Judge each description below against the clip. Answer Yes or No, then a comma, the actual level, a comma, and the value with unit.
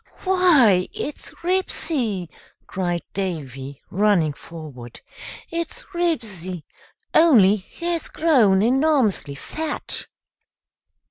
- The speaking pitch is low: No, high, 210 Hz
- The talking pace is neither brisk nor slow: No, slow, 75 wpm